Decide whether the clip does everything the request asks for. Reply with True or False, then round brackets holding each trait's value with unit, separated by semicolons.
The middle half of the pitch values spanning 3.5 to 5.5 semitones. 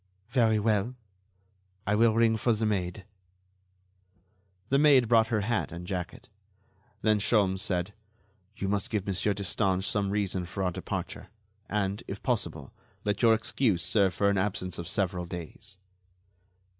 False (3.0 semitones)